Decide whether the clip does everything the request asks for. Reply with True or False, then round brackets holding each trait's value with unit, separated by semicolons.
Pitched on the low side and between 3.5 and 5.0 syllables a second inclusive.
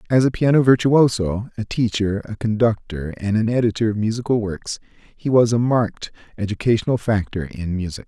False (110 Hz; 5.4 syllables/s)